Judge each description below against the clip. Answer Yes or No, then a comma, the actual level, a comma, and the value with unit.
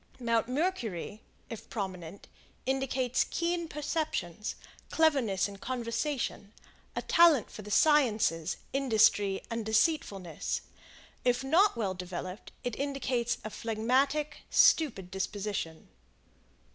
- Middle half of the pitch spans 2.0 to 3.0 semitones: No, wide, 5.5 semitones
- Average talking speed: No, slow, 100 wpm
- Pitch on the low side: No, high, 230 Hz